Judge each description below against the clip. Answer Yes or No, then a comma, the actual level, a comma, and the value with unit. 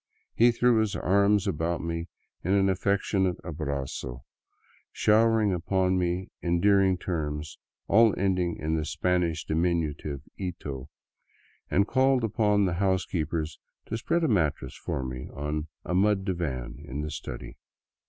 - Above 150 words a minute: No, slow, 135 wpm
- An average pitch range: Yes, average, 4.5 semitones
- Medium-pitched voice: No, very low, 90 Hz